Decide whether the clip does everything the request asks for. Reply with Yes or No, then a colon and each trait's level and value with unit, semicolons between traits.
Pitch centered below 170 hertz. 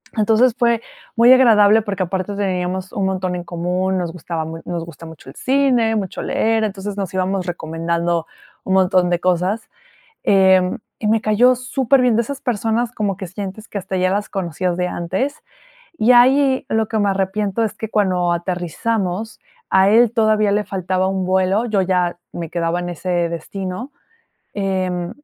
No: high, 190 Hz